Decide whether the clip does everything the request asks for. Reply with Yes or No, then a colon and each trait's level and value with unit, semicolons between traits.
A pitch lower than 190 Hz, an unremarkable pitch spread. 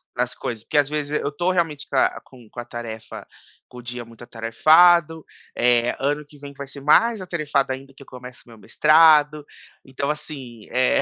Yes: medium, 140 Hz; average, 3.8 semitones